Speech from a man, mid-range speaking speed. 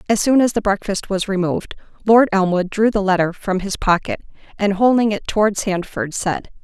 No: female; average, 190 wpm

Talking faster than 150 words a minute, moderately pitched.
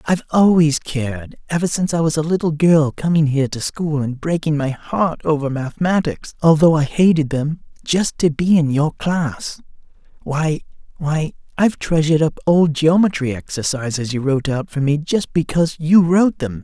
Yes: average, 160 wpm; medium, 155 Hz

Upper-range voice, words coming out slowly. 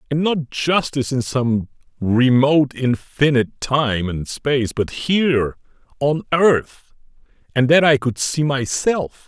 No: low, 135 Hz; slow, 130 wpm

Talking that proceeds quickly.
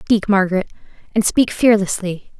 No: slow, 125 wpm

